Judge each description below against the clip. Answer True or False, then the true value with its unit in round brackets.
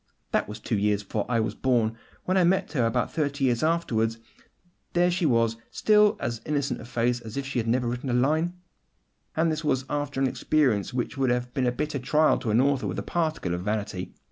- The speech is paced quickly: True (225 wpm)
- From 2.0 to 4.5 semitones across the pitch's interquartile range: False (4.9 semitones)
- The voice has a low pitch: True (130 Hz)